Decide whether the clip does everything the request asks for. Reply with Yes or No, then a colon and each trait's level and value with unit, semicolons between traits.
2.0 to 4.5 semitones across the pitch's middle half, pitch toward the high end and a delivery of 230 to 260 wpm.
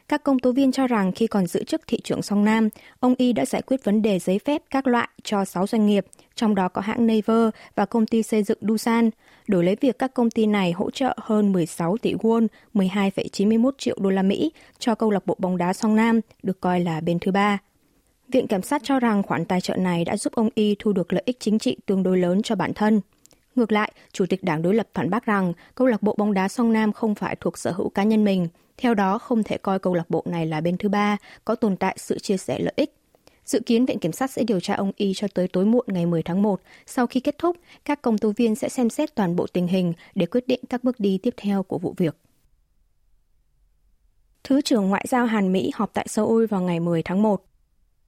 Yes: average, 3.8 semitones; high, 210 Hz; fast, 250 wpm